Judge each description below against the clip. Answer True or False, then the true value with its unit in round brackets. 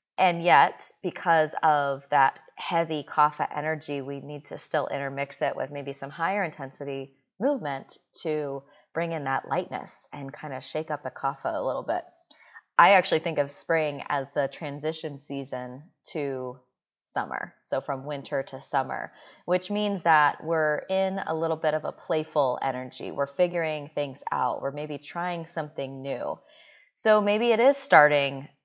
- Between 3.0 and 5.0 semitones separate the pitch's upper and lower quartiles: True (3.3 semitones)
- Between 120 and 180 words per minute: True (160 wpm)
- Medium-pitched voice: True (150 Hz)